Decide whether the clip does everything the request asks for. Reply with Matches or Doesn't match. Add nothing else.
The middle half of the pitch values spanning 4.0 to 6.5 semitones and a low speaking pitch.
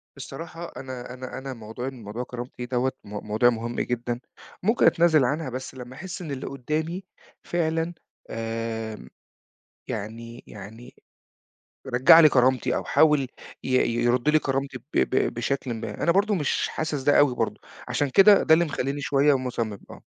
Matches